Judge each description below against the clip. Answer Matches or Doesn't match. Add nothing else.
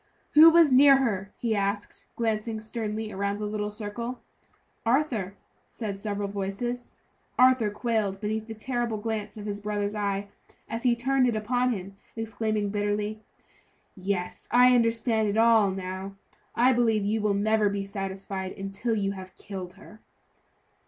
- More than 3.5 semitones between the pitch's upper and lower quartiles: Doesn't match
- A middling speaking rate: Matches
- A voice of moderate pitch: Doesn't match